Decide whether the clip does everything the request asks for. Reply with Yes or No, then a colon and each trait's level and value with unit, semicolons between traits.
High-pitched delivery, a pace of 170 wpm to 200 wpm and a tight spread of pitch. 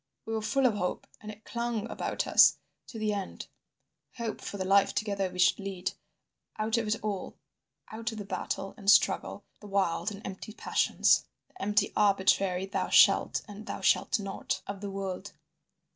Yes: high, 205 Hz; average, 180 wpm; narrow, 1.9 semitones